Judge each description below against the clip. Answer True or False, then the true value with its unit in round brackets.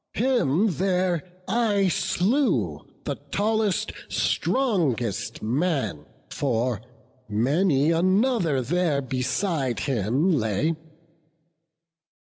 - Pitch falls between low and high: True (160 Hz)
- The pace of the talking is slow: True (75 wpm)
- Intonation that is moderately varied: False (7.5 semitones)